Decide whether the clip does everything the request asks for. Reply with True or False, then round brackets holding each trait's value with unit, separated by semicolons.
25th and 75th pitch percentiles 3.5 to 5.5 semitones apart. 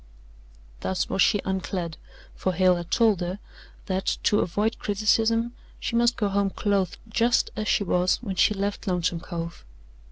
False (2.9 semitones)